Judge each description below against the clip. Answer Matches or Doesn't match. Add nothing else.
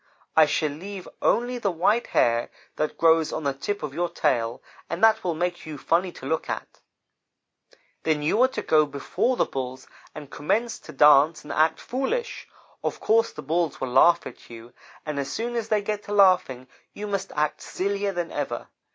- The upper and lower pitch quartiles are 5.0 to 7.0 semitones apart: Matches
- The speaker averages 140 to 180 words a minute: Doesn't match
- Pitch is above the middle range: Doesn't match